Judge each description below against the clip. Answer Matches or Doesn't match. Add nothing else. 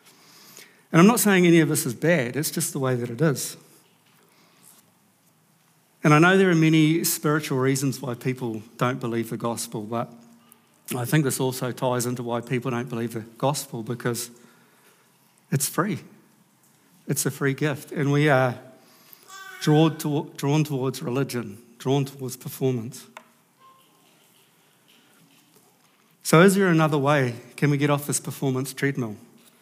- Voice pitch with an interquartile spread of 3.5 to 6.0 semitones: Matches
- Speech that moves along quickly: Doesn't match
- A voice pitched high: Doesn't match